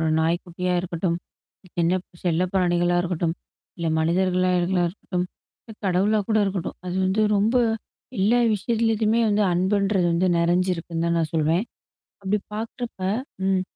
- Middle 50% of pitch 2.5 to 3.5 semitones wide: Yes, average, 2.8 semitones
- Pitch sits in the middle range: Yes, medium, 180 Hz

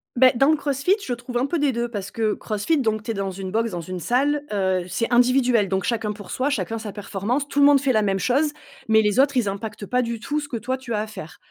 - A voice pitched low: No, high, 230 Hz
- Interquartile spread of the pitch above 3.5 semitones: Yes, average, 4.3 semitones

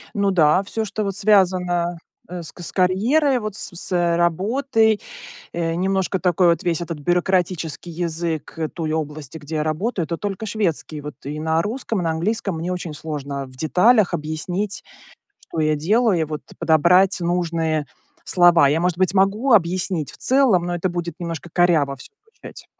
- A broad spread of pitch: No, average, 3.4 semitones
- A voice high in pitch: No, medium, 175 Hz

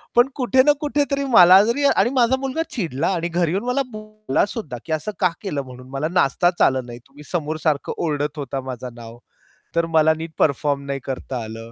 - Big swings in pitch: Yes, wide, 7.8 semitones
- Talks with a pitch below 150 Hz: No, medium, 160 Hz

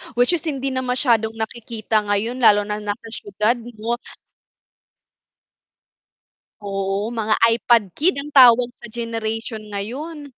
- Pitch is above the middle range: Yes, high, 230 Hz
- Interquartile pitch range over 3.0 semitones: No, average, 2.7 semitones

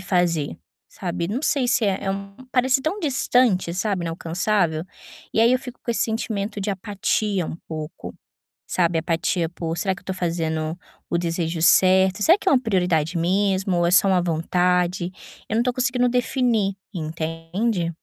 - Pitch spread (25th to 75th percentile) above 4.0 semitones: Yes, average, 4.7 semitones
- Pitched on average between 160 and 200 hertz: Yes, medium, 185 Hz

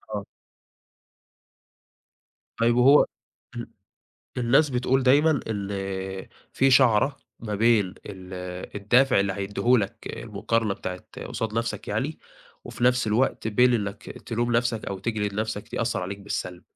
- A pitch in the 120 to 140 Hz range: No, low, 110 Hz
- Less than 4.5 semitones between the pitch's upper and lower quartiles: Yes, average, 3.7 semitones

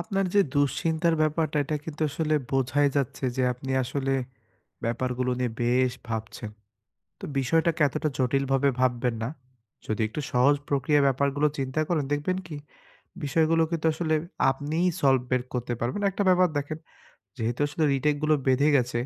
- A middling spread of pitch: Yes, average, 3.5 semitones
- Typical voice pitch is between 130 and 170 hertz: Yes, medium, 140 Hz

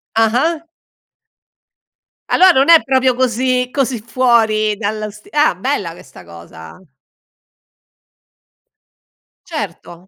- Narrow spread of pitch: No, average, 4.4 semitones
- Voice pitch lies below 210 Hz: No, high, 230 Hz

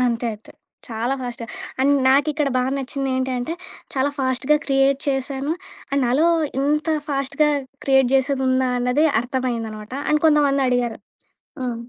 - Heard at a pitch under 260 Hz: No, very high, 265 Hz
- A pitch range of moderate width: No, narrow, 2.1 semitones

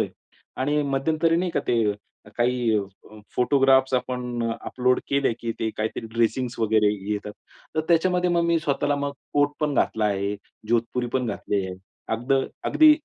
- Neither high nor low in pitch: No, low, 125 Hz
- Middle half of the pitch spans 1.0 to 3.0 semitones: No, average, 4.3 semitones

